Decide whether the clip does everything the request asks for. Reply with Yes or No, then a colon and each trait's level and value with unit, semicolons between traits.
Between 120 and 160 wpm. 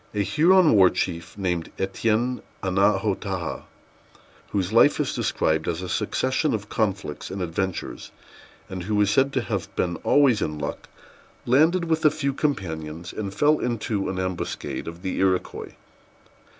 Yes: average, 150 wpm